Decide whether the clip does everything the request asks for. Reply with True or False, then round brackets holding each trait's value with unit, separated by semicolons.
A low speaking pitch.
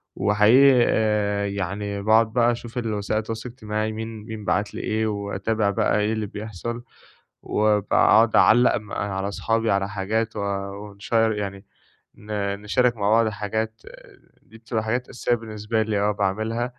True (110 Hz)